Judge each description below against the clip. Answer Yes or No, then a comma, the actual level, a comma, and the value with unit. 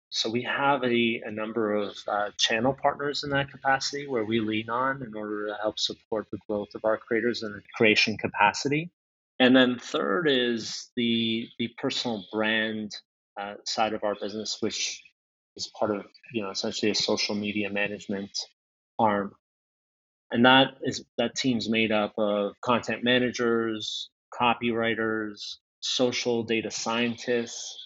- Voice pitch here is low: Yes, low, 115 Hz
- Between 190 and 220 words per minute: No, average, 150 wpm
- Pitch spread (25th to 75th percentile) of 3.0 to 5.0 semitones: No, narrow, 2.6 semitones